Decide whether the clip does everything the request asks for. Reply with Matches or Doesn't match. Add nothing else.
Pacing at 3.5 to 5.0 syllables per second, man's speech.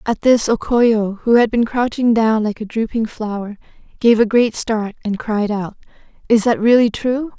Doesn't match